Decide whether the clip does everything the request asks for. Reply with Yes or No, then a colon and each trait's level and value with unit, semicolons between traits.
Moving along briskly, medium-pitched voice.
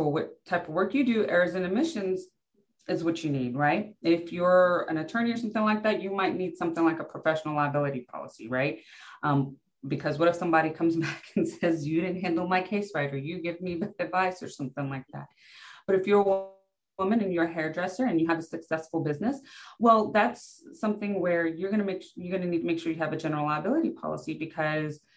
Yes: fast, 215 wpm; medium, 175 Hz